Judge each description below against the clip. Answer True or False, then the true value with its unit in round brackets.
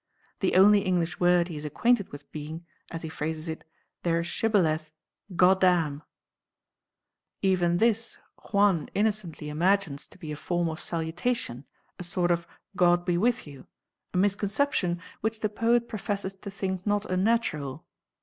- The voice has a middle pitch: True (180 Hz)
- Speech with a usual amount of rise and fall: True (3.9 semitones)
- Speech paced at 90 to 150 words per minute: True (145 wpm)